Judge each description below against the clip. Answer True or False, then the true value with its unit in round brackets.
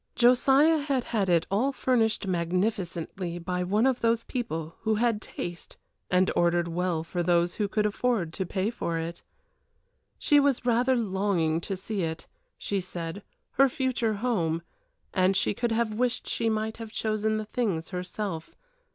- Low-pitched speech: False (205 Hz)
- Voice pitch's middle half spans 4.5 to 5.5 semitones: True (5.0 semitones)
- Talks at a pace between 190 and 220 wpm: False (160 wpm)